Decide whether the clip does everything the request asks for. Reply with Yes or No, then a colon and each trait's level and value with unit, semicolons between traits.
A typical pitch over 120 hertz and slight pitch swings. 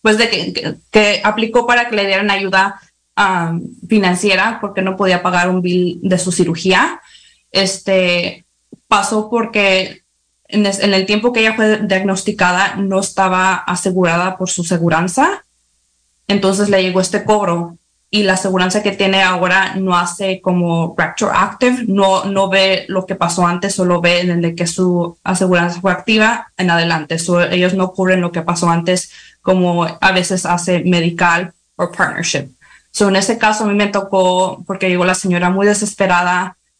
Yes: medium, 185 Hz; narrow, 2.1 semitones